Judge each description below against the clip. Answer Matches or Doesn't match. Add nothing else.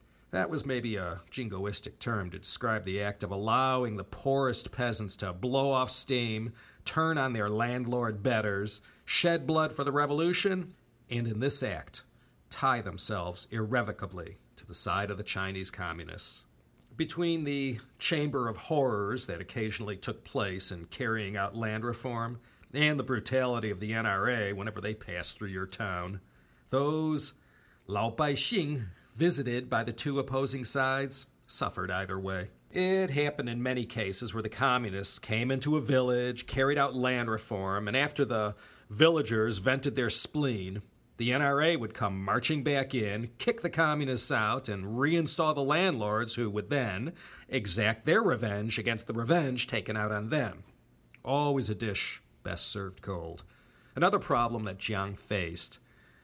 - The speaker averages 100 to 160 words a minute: Matches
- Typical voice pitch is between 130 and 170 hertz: Doesn't match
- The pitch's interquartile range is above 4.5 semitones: Matches